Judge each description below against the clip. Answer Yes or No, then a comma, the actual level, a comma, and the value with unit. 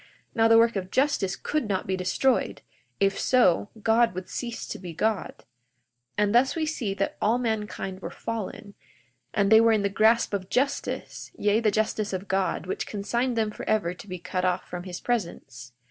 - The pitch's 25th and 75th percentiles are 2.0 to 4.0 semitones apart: Yes, average, 3.4 semitones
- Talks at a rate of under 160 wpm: No, average, 190 wpm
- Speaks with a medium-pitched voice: No, high, 210 Hz